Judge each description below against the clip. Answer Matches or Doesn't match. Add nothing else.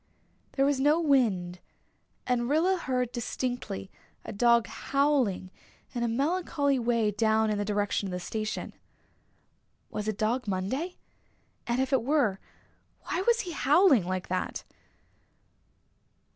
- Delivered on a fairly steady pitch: Doesn't match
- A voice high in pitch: Matches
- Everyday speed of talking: Doesn't match